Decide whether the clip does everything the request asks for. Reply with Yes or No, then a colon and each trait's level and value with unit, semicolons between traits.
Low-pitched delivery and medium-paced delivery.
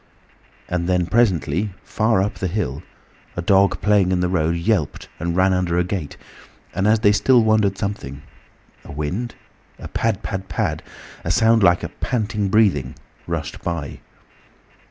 Yes: very low, 95 Hz; average, 145 wpm